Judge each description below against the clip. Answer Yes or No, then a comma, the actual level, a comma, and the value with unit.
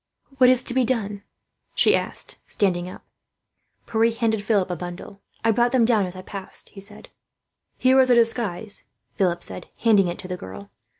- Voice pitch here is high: Yes, high, 205 Hz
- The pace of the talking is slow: No, average, 185 wpm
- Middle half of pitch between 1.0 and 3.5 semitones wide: No, average, 4.2 semitones